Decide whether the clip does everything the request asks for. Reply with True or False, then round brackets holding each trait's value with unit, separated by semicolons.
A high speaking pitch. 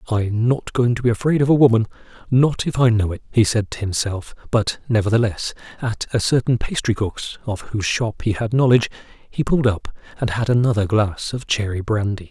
False (115 Hz)